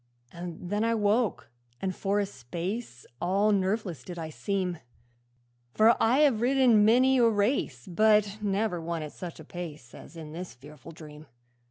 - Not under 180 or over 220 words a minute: No, average, 165 wpm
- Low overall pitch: No, high, 190 Hz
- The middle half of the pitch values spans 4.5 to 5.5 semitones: Yes, average, 4.8 semitones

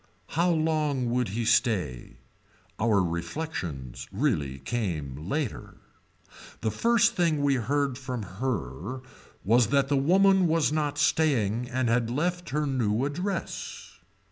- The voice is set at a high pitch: No, low, 130 Hz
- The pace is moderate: No, slow, 125 wpm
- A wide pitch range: Yes, wide, 6.6 semitones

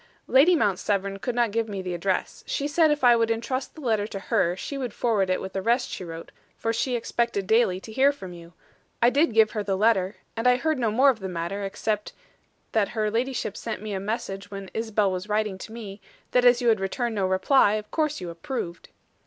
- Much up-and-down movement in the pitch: No, average, 3.9 semitones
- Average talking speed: No, fast, 235 wpm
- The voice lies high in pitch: Yes, high, 215 Hz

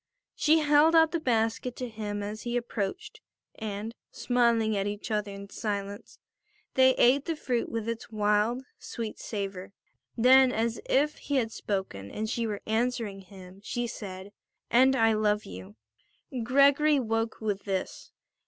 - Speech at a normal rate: Yes, average, 155 wpm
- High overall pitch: Yes, high, 225 Hz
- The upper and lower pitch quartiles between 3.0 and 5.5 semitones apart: Yes, average, 3.5 semitones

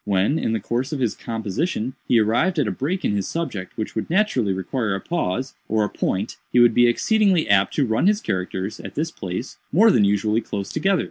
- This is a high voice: No, low, 115 Hz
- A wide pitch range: Yes, wide, 7.4 semitones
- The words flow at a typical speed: No, fast, 220 wpm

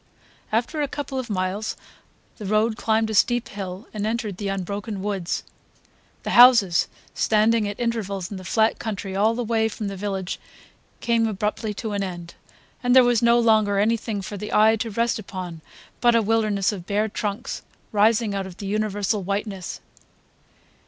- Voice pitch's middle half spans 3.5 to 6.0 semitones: No, narrow, 2.4 semitones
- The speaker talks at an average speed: Yes, average, 170 wpm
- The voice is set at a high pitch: Yes, high, 210 Hz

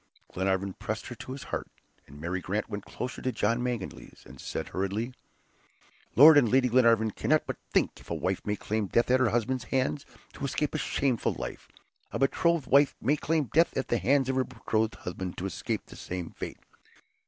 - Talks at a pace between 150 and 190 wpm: No, average, 200 wpm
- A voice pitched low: Yes, low, 120 Hz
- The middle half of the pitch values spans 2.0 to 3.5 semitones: No, average, 4.3 semitones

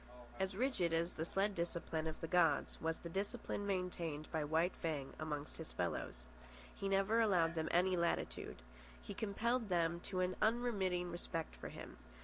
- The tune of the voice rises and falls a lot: No, average, 3.2 semitones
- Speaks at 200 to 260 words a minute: No, average, 165 wpm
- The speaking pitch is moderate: Yes, medium, 175 Hz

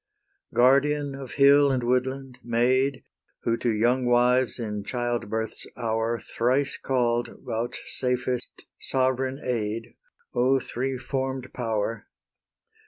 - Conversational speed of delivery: No, slow, 105 wpm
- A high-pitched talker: No, low, 125 Hz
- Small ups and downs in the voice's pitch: Yes, narrow, 2.0 semitones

